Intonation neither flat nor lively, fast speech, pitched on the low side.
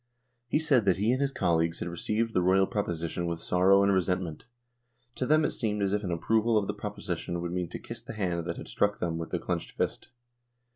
Yes: average, 4.1 semitones; fast, 230 wpm; very low, 95 Hz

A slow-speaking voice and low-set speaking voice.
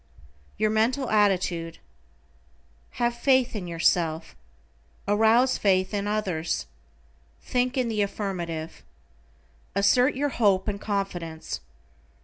No: slow, 100 wpm; high, 205 Hz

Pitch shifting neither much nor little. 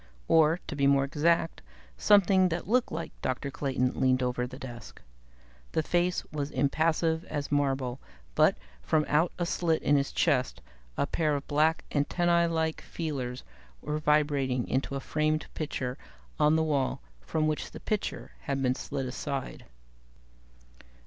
Yes: average, 3.1 semitones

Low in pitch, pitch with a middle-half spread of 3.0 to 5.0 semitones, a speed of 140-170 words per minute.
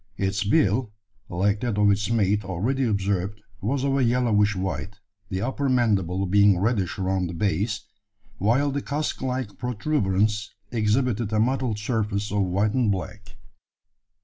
Yes: low, 105 Hz; average, 3.7 semitones; average, 150 wpm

